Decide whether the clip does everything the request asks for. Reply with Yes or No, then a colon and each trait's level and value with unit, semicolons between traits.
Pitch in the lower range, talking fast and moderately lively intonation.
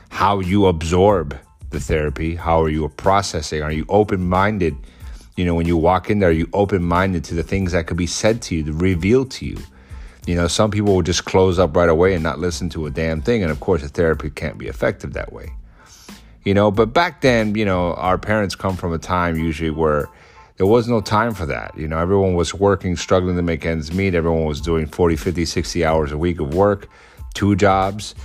Yes: very low, 90 Hz; fast, 225 wpm; average, 3.4 semitones